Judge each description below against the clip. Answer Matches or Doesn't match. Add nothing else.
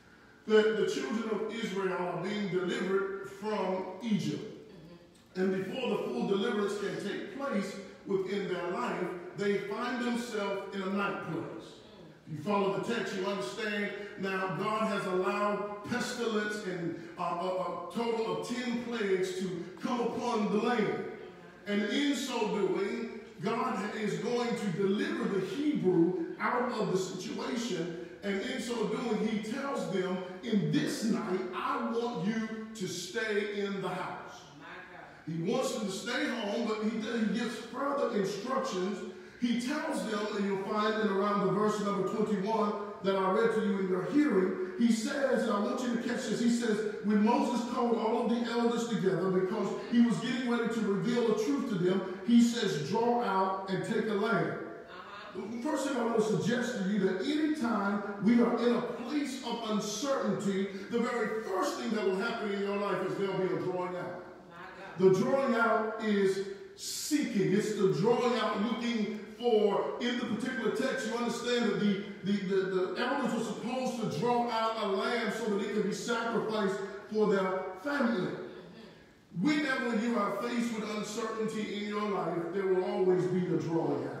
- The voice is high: Matches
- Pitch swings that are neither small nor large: Matches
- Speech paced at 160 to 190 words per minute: Matches